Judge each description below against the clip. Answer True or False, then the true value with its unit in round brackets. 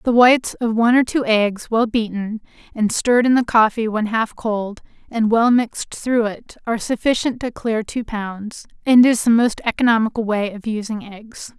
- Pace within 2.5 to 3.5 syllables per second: False (4.9 syllables/s)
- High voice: True (225 Hz)